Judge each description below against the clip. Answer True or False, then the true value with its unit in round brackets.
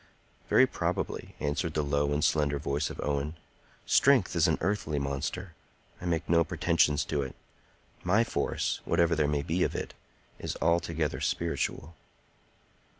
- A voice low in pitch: True (80 Hz)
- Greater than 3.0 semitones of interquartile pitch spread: False (2.7 semitones)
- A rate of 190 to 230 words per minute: False (150 wpm)